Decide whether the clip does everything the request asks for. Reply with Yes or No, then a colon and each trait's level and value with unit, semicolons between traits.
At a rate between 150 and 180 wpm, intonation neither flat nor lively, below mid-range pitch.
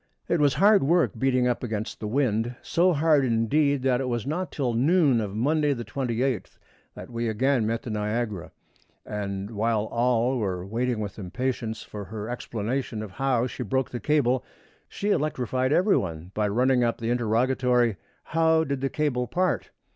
Yes: average, 175 wpm; average, 3.8 semitones; low, 125 Hz